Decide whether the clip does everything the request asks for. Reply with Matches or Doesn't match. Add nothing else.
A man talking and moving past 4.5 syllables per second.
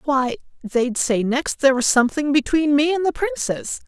Doesn't match